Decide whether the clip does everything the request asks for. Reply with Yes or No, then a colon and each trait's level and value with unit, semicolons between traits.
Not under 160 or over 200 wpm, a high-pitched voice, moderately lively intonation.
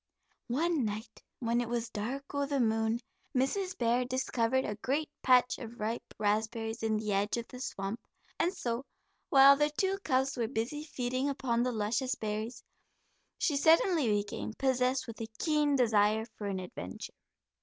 Yes: average, 165 wpm; high, 245 Hz; average, 3.6 semitones